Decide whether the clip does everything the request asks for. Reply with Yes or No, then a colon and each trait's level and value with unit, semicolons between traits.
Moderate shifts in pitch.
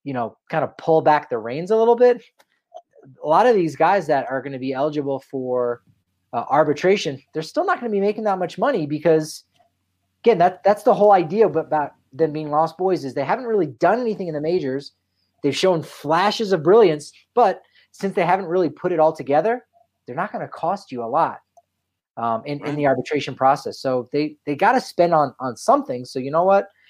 No: wide, 6.1 semitones